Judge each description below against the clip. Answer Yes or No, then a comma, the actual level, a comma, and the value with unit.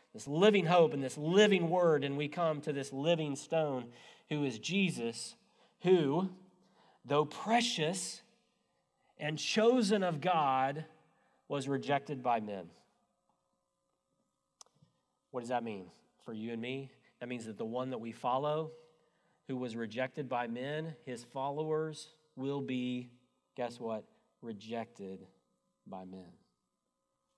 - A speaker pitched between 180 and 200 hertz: No, medium, 140 Hz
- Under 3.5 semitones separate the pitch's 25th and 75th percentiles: No, average, 5.0 semitones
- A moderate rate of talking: No, slow, 125 wpm